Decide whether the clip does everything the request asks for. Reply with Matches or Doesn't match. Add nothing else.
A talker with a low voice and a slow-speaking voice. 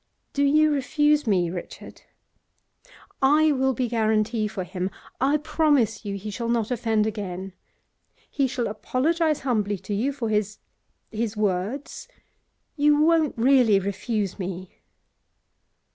Doesn't match